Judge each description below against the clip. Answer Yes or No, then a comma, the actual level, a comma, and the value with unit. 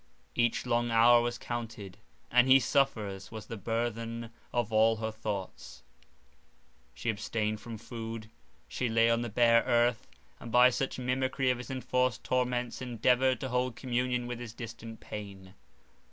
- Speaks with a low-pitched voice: Yes, low, 120 Hz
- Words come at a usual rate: Yes, average, 155 wpm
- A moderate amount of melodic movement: No, narrow, 1.8 semitones